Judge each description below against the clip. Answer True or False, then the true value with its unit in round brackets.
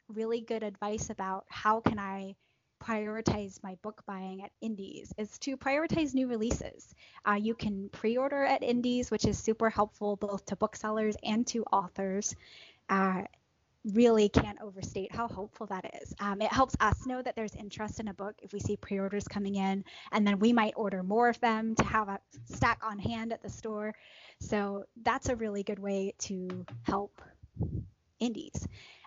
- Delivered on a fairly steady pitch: True (2.3 semitones)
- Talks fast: False (175 wpm)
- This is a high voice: True (215 Hz)